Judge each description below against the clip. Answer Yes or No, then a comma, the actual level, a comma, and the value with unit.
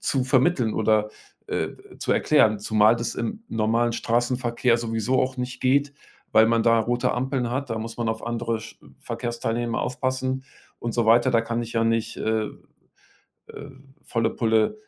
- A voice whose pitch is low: Yes, low, 115 Hz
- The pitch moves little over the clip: Yes, narrow, 2.1 semitones